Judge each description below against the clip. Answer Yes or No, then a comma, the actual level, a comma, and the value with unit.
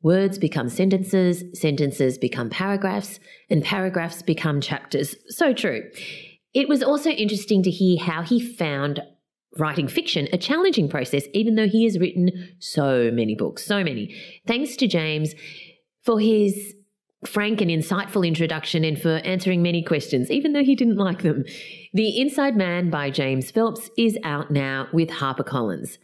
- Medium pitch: Yes, medium, 180 Hz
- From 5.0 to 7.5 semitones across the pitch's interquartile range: Yes, wide, 5.4 semitones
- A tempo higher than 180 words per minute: No, average, 155 wpm